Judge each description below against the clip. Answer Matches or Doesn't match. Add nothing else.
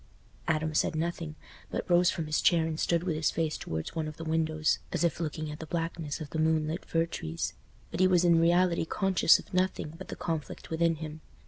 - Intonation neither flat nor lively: Doesn't match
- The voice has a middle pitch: Matches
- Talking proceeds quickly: Matches